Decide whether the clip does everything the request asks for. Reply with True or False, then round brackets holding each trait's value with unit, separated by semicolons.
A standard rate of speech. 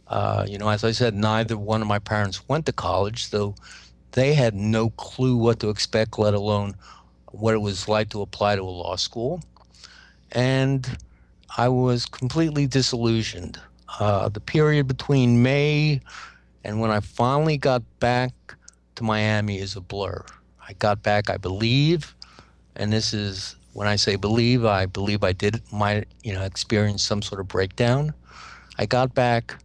True (165 wpm)